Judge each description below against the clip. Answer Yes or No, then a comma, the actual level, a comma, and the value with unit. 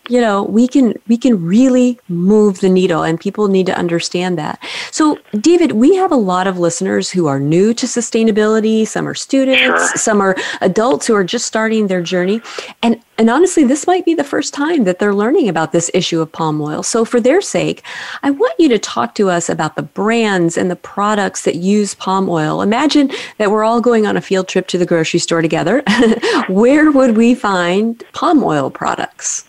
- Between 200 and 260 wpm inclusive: Yes, fast, 205 wpm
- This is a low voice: No, high, 210 Hz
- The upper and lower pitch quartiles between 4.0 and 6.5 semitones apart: Yes, average, 5.1 semitones